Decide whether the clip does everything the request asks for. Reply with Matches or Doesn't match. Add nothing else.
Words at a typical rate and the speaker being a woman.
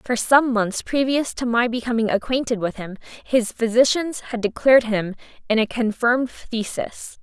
Matches